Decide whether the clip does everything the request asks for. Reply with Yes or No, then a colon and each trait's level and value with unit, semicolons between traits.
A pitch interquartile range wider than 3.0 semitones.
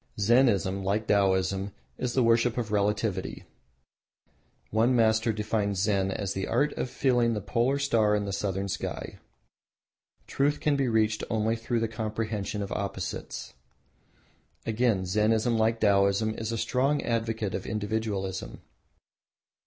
No: narrow, 2.5 semitones